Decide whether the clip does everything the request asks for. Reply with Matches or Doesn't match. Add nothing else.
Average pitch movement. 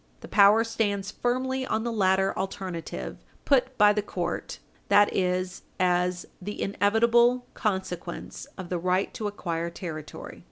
Matches